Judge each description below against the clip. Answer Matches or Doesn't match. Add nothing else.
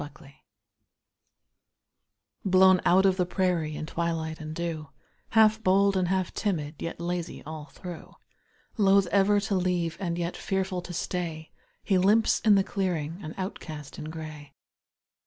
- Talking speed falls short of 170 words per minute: Matches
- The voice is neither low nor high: Matches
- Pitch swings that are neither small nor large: Matches